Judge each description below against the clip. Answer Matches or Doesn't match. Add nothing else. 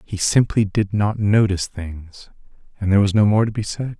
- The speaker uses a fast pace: Matches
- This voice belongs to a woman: Doesn't match